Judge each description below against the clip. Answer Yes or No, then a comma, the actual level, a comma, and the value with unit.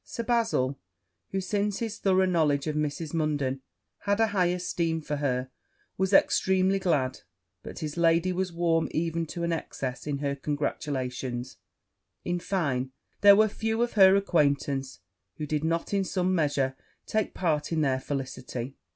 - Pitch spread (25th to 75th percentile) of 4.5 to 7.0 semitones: Yes, average, 5.0 semitones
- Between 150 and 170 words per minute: Yes, average, 160 wpm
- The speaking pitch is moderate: Yes, medium, 165 Hz